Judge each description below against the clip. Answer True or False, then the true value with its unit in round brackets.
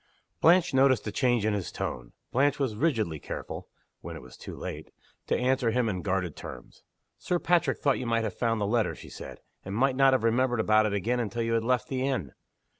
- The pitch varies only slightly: False (3.7 semitones)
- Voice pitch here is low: True (120 Hz)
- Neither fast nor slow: False (225 wpm)